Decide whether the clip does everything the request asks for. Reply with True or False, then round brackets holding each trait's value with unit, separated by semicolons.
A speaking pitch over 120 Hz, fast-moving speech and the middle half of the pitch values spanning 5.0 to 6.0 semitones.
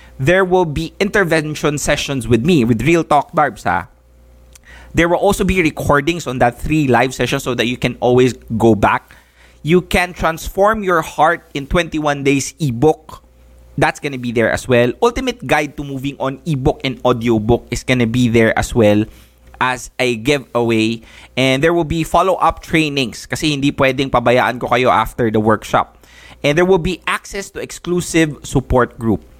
False (140 Hz; 170 wpm; 5.3 semitones)